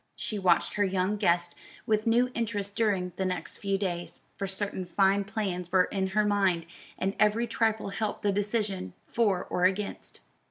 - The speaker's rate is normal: Yes, average, 170 wpm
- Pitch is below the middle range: No, high, 200 Hz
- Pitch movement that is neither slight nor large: No, narrow, 2.3 semitones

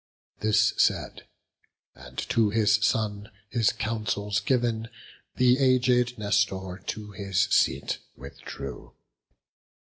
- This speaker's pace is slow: Yes, slow, 95 wpm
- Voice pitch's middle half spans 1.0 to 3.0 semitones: Yes, narrow, 2.4 semitones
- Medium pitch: No, low, 110 Hz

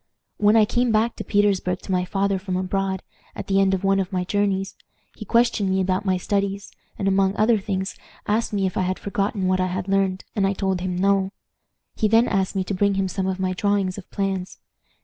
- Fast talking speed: Yes, fast, 225 wpm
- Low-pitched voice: No, high, 195 Hz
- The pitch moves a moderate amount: No, narrow, 1.4 semitones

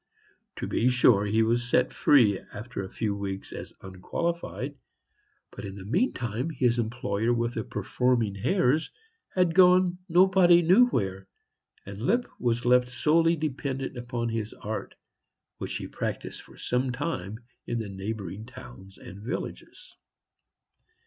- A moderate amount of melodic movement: No, wide, 6.7 semitones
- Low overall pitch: Yes, low, 120 Hz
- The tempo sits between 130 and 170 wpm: Yes, average, 140 wpm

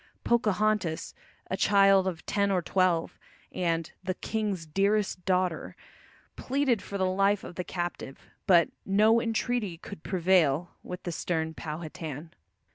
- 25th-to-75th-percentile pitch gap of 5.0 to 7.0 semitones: No, average, 3.3 semitones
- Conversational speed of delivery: No, slow, 130 wpm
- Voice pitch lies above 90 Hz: Yes, medium, 185 Hz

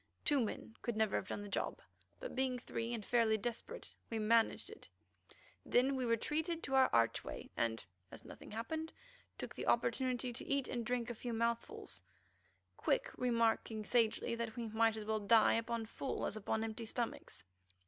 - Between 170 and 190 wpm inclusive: Yes, average, 175 wpm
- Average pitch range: No, narrow, 2.3 semitones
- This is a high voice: Yes, high, 230 Hz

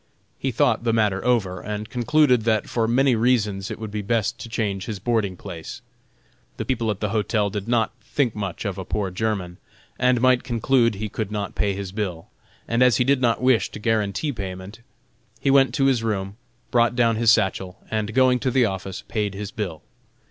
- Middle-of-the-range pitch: No, low, 110 Hz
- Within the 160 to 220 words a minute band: Yes, average, 200 wpm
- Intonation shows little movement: No, average, 3.3 semitones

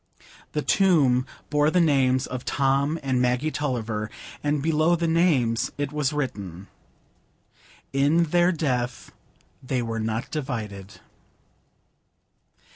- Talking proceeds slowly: Yes, slow, 115 wpm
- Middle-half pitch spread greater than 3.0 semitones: Yes, average, 3.9 semitones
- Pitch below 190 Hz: Yes, low, 135 Hz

